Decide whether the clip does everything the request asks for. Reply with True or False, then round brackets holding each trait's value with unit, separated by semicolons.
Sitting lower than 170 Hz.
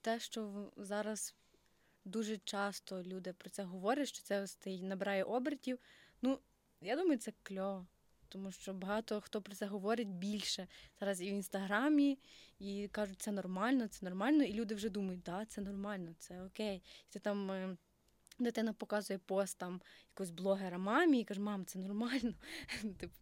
False (205 Hz)